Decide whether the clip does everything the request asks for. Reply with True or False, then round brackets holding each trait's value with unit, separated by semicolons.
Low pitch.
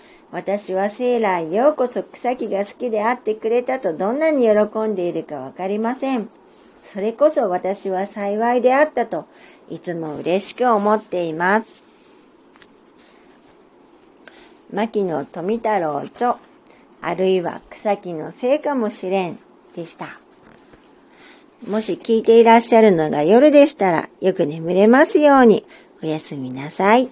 False (215 Hz)